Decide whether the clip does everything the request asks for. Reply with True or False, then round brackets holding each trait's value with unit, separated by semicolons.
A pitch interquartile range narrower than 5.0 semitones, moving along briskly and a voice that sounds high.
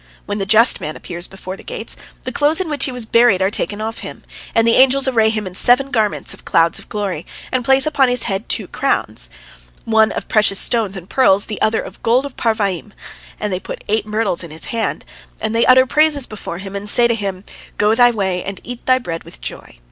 True (4.1 semitones; 230 wpm; 220 Hz)